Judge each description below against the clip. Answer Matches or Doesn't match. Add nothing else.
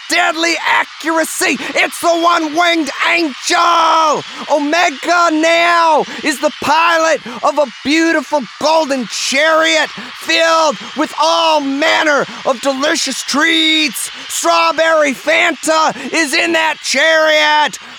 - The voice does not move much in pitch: Matches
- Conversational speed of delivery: Doesn't match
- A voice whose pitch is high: Matches